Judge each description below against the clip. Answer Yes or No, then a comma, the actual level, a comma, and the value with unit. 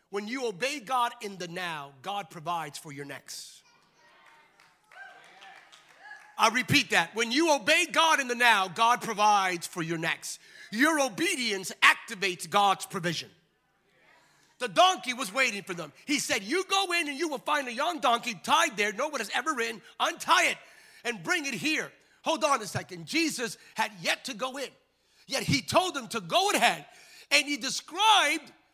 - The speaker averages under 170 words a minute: No, average, 175 wpm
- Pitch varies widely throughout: Yes, wide, 7.2 semitones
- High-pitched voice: Yes, very high, 250 Hz